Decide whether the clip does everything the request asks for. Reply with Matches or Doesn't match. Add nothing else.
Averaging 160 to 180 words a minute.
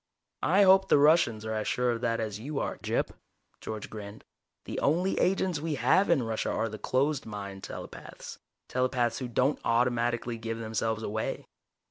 Matches